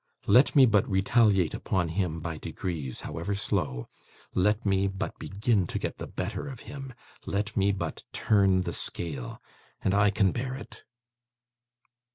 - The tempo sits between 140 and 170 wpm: Yes, average, 155 wpm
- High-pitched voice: No, low, 100 Hz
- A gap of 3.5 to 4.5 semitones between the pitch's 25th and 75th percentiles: No, average, 2.9 semitones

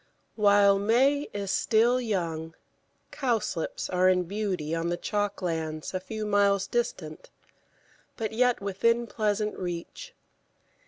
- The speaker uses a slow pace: Yes, slow, 120 wpm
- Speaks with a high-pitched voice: Yes, high, 200 Hz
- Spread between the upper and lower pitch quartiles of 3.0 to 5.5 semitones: Yes, average, 3.8 semitones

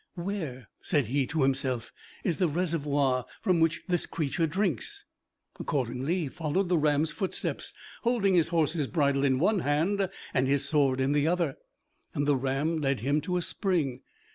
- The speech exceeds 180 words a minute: No, average, 165 wpm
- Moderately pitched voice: Yes, medium, 150 Hz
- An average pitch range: Yes, average, 4.1 semitones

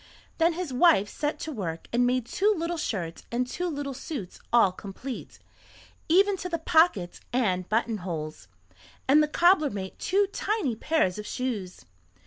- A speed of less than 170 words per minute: Yes, average, 155 wpm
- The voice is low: No, very high, 255 Hz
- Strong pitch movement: Yes, wide, 8.7 semitones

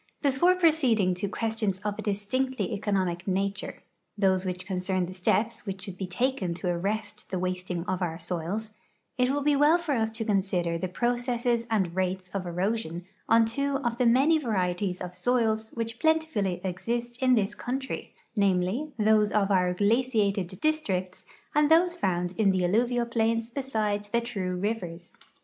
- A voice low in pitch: No, high, 210 Hz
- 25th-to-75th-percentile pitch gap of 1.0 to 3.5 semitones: No, average, 4.6 semitones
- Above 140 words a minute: Yes, average, 170 wpm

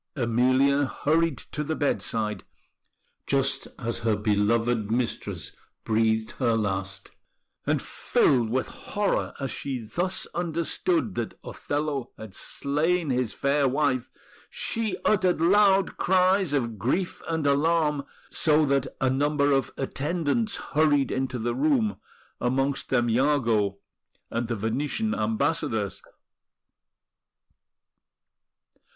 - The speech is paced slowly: Yes, slow, 110 wpm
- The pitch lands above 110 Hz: Yes, low, 135 Hz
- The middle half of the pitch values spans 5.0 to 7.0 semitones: Yes, average, 5.3 semitones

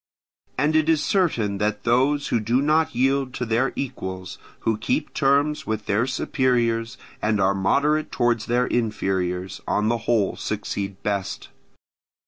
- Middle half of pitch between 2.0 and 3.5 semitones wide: No, average, 4.7 semitones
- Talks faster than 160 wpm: No, average, 145 wpm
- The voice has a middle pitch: No, low, 120 Hz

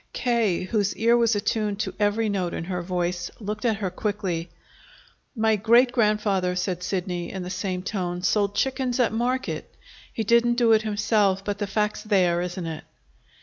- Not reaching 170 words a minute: No, average, 175 wpm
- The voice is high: Yes, high, 205 Hz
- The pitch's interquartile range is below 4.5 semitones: Yes, average, 3.5 semitones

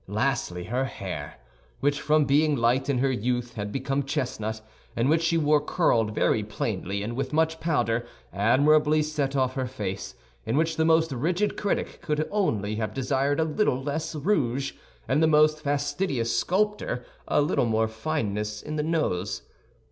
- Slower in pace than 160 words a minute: No, average, 165 wpm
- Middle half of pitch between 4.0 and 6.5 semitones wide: Yes, average, 4.8 semitones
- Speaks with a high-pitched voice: No, medium, 140 Hz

